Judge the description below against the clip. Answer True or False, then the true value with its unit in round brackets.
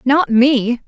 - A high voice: True (255 Hz)